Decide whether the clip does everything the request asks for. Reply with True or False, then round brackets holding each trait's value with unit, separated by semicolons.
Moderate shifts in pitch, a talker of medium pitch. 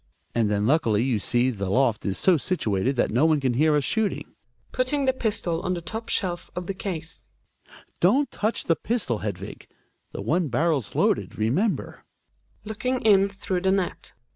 False (8.5 semitones; 165 Hz)